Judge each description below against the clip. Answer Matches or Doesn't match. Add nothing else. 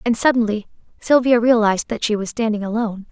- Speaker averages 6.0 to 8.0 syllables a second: Matches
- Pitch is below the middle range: Doesn't match